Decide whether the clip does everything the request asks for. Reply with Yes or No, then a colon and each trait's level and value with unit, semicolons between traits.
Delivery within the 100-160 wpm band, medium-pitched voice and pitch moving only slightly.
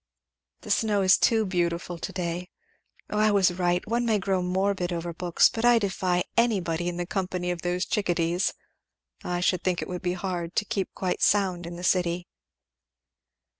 No: average, 190 wpm; medium, 180 Hz; narrow, 2.0 semitones